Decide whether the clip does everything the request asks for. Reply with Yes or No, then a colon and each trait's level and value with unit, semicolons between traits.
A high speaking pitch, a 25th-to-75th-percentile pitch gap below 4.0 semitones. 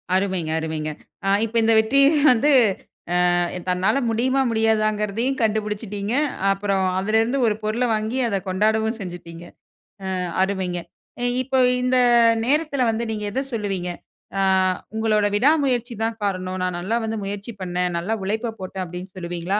Yes: high, 210 Hz; average, 3.3 semitones